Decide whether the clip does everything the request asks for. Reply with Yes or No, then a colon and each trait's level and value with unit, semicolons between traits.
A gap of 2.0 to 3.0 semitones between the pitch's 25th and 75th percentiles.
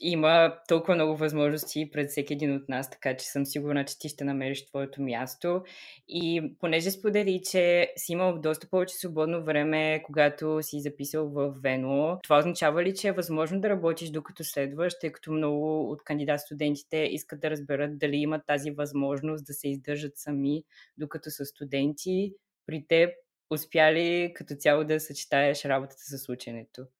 Yes: narrow, 2.6 semitones